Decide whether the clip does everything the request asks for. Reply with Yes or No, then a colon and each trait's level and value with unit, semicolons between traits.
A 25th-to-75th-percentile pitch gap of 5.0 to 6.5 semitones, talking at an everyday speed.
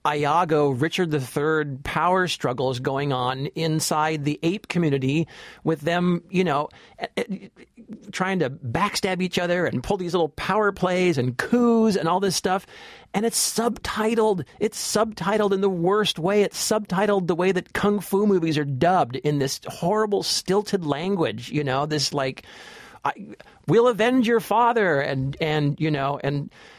Yes: wide, 5.4 semitones; average, 155 wpm